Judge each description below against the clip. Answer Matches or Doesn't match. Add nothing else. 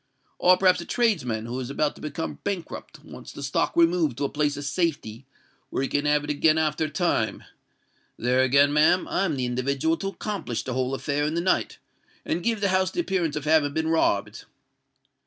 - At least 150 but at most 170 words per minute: Doesn't match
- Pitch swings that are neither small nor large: Matches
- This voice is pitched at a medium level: Matches